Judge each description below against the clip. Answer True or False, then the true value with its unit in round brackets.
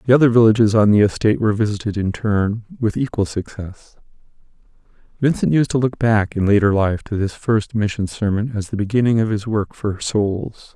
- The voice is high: False (105 Hz)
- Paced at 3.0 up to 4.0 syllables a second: False (5.4 syllables/s)